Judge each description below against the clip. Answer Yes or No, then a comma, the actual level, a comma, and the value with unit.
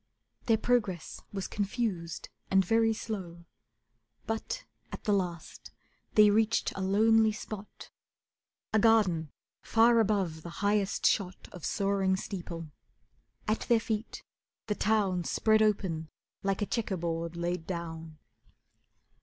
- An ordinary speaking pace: No, slow, 120 wpm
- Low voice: No, high, 200 Hz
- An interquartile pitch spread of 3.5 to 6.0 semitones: Yes, average, 4.1 semitones